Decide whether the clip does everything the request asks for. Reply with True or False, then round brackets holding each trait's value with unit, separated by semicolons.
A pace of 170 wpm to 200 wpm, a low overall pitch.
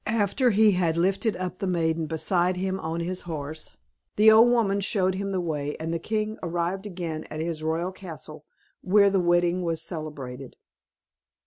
False (175 wpm; 175 Hz)